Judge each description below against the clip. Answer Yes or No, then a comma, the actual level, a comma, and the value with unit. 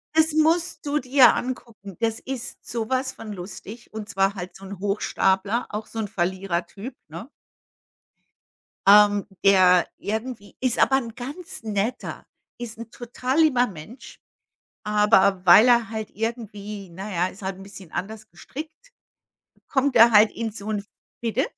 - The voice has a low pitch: No, high, 220 Hz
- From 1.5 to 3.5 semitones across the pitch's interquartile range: No, average, 4.0 semitones